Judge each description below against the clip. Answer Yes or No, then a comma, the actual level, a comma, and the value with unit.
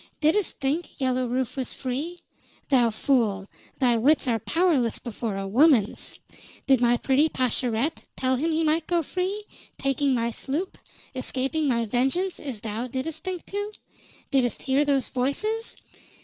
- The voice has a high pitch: Yes, very high, 265 Hz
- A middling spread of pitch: Yes, average, 4.6 semitones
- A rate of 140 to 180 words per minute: Yes, average, 150 wpm